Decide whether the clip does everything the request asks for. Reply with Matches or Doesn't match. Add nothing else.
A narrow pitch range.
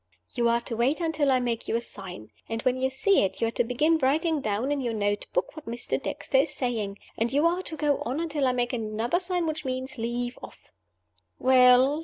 Doesn't match